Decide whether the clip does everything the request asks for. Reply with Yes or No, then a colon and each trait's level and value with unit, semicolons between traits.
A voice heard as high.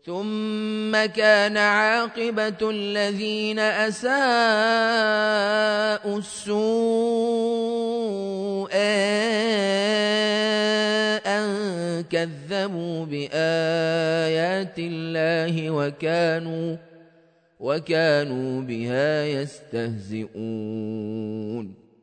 Yes: high, 195 Hz